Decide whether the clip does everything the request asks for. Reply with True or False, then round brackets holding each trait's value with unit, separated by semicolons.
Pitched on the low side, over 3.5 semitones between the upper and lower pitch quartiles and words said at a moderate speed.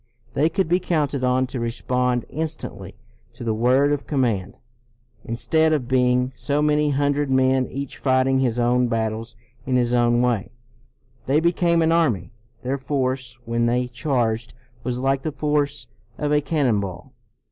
False (130 Hz; 3.2 semitones; 160 wpm)